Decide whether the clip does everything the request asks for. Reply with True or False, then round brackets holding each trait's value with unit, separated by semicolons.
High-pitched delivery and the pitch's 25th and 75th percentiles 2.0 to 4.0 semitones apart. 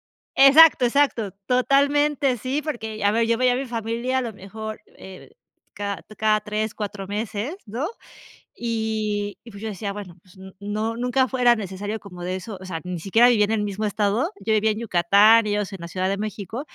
True (215 Hz; 3.1 semitones)